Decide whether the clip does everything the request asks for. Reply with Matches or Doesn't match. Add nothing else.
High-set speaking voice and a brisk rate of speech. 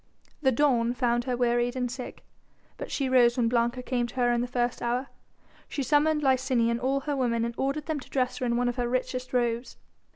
Matches